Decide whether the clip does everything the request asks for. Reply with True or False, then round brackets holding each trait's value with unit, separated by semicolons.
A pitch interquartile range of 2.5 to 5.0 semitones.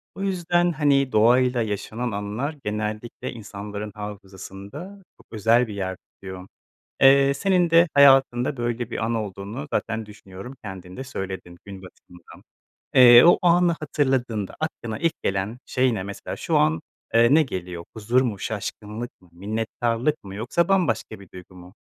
False (5.4 semitones)